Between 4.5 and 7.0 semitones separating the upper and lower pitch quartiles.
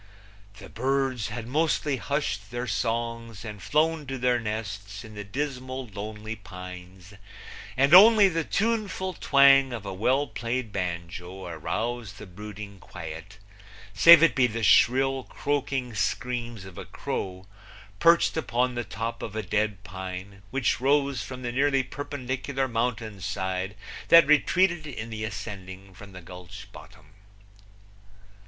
Yes: average, 5.2 semitones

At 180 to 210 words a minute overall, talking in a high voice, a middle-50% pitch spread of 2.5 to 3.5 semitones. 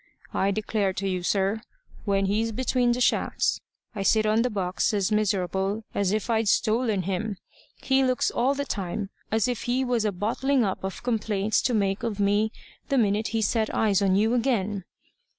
Yes: average, 185 wpm; high, 215 Hz; average, 2.9 semitones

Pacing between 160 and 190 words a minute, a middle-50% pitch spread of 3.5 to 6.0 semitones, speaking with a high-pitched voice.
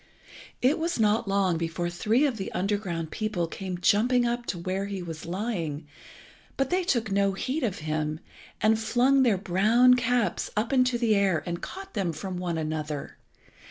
Yes: average, 175 wpm; wide, 5.6 semitones; high, 200 Hz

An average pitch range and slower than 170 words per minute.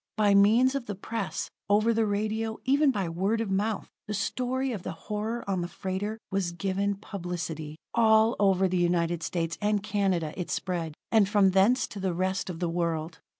No: average, 3.6 semitones; average, 190 wpm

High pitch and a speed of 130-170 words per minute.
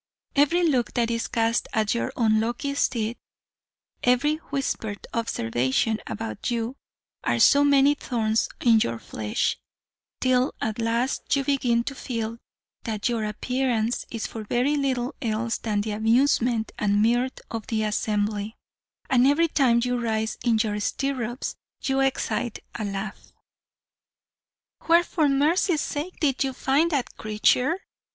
Yes: high, 235 Hz; average, 140 wpm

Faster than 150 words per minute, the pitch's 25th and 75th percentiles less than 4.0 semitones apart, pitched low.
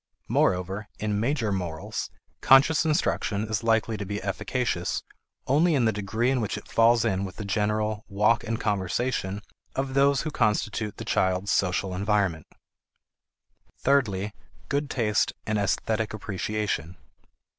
No: slow, 135 wpm; average, 3.2 semitones; low, 105 Hz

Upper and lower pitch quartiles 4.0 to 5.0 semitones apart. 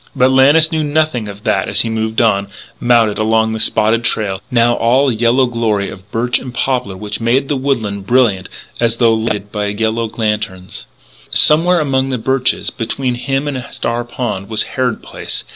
No: average, 3.3 semitones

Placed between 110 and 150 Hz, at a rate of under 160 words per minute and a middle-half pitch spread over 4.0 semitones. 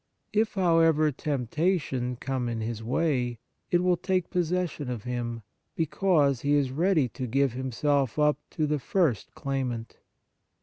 Yes: medium, 140 Hz; average, 140 wpm; average, 5.0 semitones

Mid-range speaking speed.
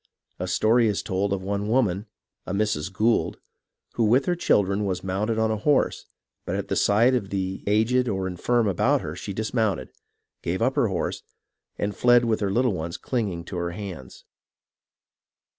Yes: average, 175 wpm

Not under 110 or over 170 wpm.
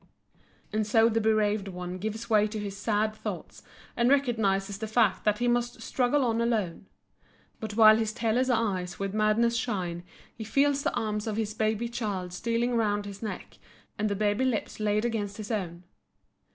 No: average, 180 wpm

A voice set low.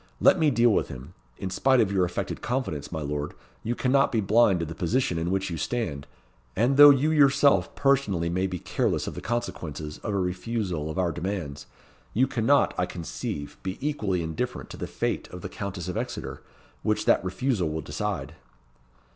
Yes: very low, 95 Hz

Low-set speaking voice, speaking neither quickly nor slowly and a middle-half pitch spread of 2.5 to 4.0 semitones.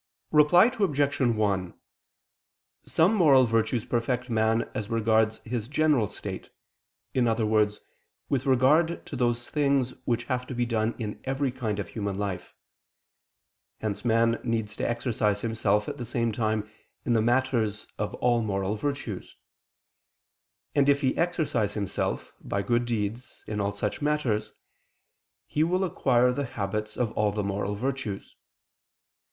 Yes: low, 115 Hz; average, 145 wpm; average, 3.7 semitones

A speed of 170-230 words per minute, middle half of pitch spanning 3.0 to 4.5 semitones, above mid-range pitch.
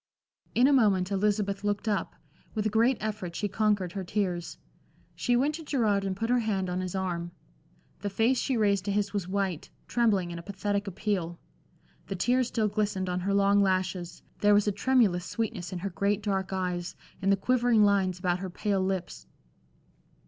No: average, 190 wpm; narrow, 2.5 semitones; high, 200 Hz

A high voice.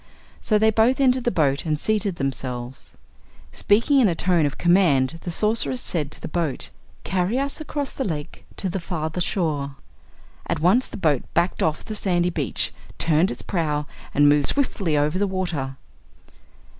No: medium, 175 Hz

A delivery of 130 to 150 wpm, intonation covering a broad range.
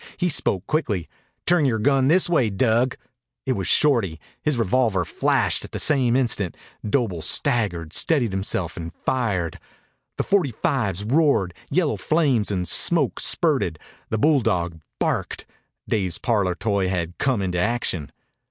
Yes: average, 145 wpm; wide, 6.8 semitones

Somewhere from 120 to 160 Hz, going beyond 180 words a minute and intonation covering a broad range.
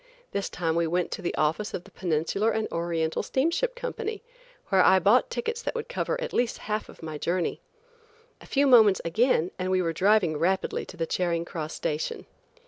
No: medium, 185 Hz; average, 195 wpm; wide, 6.9 semitones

